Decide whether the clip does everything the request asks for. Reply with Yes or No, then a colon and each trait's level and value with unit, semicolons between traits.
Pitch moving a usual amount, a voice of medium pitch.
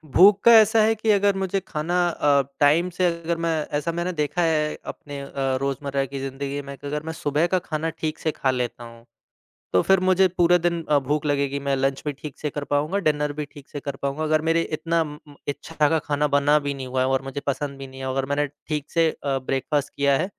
Yes: average, 3.2 semitones; medium, 150 Hz